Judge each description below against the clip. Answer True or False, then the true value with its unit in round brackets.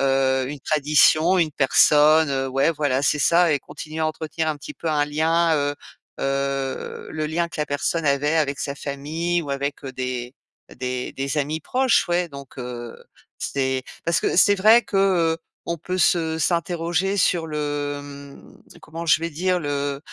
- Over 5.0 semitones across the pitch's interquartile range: False (3.2 semitones)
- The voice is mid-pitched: True (150 Hz)